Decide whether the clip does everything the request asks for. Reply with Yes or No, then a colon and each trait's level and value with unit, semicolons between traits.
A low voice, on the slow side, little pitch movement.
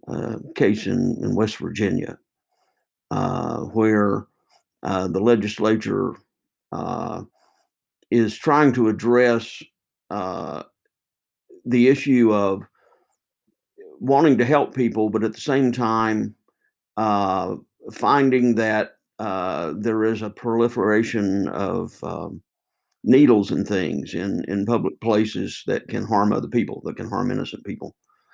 Yes: low, 110 Hz; slow, 120 wpm; narrow, 2.3 semitones